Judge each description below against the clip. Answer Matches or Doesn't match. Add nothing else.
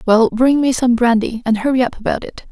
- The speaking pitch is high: Matches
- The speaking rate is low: Doesn't match